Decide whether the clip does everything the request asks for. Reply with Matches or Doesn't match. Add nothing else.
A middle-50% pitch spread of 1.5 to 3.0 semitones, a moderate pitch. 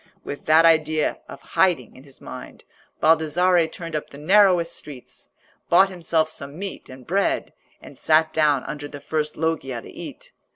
Matches